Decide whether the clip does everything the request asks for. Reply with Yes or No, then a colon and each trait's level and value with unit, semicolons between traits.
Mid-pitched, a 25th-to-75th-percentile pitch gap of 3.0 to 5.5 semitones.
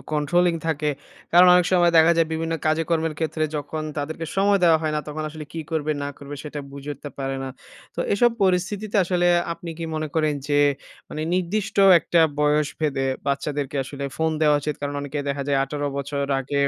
No: medium, 155 Hz; narrow, 2.6 semitones